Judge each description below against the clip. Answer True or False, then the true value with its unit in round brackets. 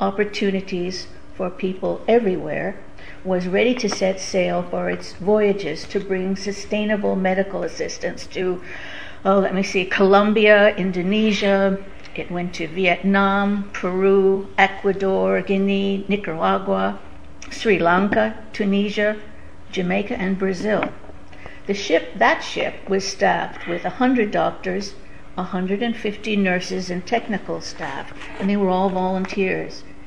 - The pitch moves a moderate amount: False (2.0 semitones)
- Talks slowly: True (120 wpm)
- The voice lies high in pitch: True (195 Hz)